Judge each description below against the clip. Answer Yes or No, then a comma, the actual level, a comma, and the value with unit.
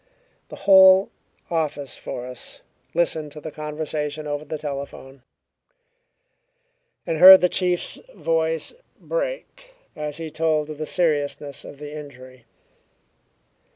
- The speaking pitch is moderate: Yes, medium, 155 Hz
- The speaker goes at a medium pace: No, slow, 115 wpm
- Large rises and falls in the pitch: No, narrow, 2.4 semitones